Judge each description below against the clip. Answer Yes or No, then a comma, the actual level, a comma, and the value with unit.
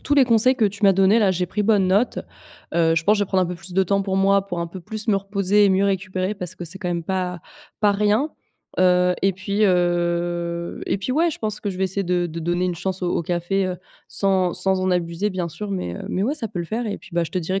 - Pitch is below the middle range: No, high, 190 Hz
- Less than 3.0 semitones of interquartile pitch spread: Yes, narrow, 2.4 semitones